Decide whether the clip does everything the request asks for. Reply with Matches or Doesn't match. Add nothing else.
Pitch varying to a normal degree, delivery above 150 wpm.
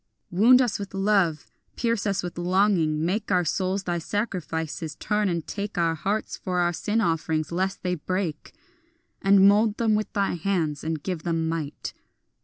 Matches